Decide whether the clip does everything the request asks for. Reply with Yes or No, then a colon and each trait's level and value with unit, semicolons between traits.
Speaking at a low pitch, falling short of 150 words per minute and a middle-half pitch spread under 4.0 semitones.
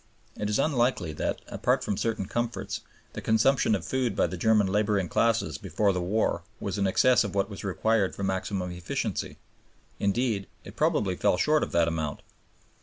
No: low, 100 Hz; average, 180 wpm; average, 3.4 semitones